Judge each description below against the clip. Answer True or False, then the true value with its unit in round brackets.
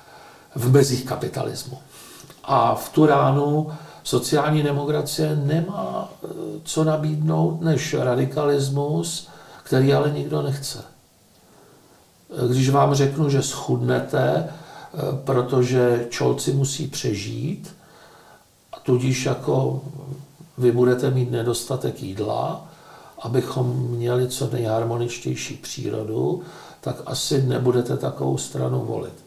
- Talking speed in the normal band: False (95 wpm)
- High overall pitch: False (135 Hz)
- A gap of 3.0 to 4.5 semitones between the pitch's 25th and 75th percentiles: True (3.5 semitones)